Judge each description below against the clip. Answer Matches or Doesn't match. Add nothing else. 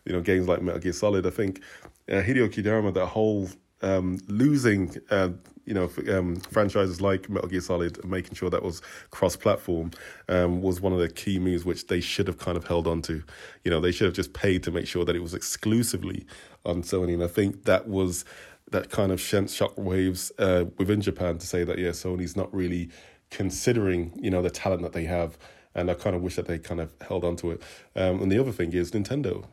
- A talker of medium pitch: Doesn't match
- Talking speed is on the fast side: Matches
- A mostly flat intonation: Matches